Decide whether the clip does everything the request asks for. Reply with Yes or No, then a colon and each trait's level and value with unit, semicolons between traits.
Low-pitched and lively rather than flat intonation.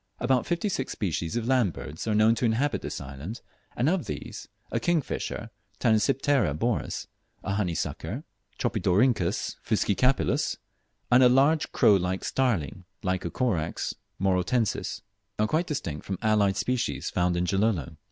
Yes: low, 110 Hz; wide, 5.7 semitones